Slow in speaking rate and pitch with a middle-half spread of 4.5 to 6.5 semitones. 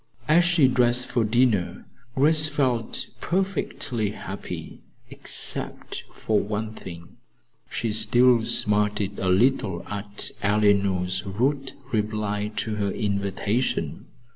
No: slow, 105 wpm; average, 3.7 semitones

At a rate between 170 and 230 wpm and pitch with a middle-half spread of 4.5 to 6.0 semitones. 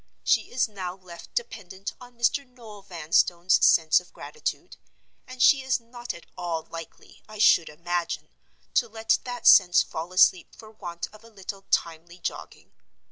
No: average, 160 wpm; average, 5.3 semitones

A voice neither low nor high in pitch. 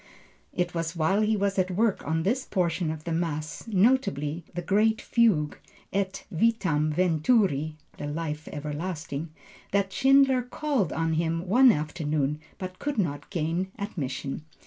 Yes: medium, 175 Hz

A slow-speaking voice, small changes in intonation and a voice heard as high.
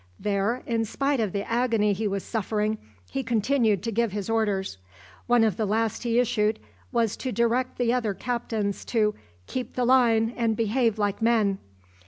No: average, 175 wpm; narrow, 2.3 semitones; high, 225 Hz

